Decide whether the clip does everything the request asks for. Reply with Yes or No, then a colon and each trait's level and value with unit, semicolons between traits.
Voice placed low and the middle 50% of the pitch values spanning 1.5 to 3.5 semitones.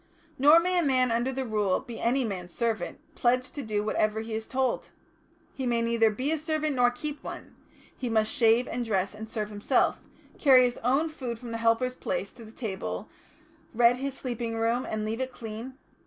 No: high, 240 Hz; average, 2.9 semitones